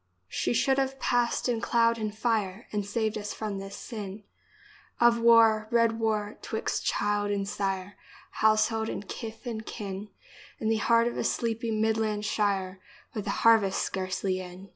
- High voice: Yes, high, 215 Hz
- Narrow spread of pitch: Yes, narrow, 2.1 semitones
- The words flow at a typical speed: Yes, average, 170 wpm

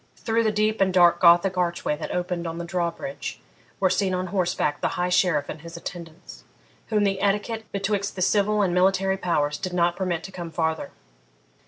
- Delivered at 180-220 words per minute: Yes, average, 190 wpm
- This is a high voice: No, medium, 180 Hz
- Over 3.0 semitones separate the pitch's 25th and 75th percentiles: No, narrow, 2.5 semitones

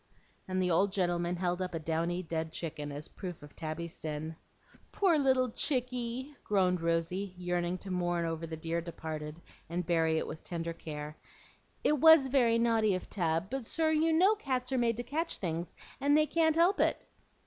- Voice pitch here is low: No, medium, 180 Hz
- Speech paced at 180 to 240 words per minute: Yes, average, 185 wpm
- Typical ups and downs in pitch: No, wide, 7.4 semitones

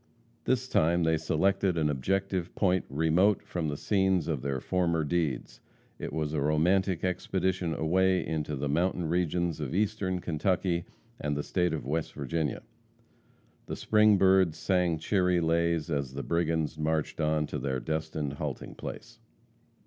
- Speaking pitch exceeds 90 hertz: No, very low, 85 Hz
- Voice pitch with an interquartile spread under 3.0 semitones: No, average, 3.3 semitones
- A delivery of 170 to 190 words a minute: No, average, 150 wpm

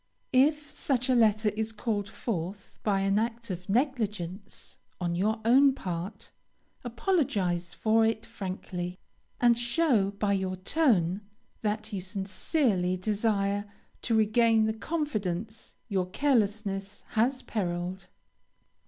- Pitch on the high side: Yes, high, 210 Hz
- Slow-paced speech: Yes, slow, 120 wpm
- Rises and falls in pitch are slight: No, average, 3.5 semitones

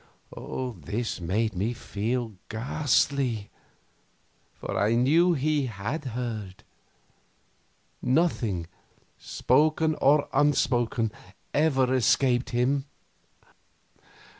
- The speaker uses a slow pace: Yes, slow, 75 wpm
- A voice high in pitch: No, low, 125 Hz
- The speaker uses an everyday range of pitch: Yes, average, 4.1 semitones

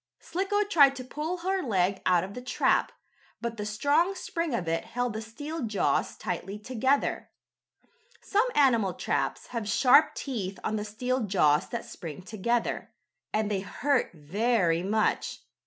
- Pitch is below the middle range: No, high, 230 Hz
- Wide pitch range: Yes, wide, 6.1 semitones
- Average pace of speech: Yes, average, 155 wpm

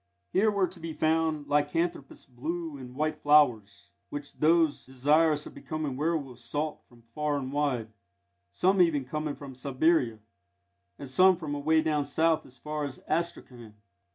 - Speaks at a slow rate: No, average, 155 wpm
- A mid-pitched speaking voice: Yes, medium, 150 Hz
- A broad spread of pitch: No, average, 3.4 semitones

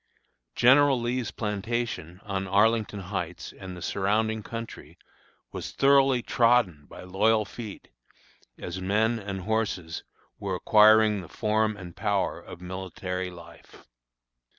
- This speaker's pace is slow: Yes, slow, 120 wpm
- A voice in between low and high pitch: No, low, 105 Hz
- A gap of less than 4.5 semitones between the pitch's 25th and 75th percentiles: Yes, average, 3.4 semitones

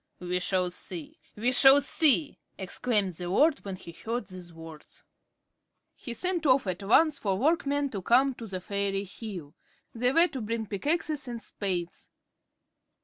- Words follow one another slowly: No, average, 155 wpm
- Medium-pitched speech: No, high, 215 Hz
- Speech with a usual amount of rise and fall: No, wide, 6.8 semitones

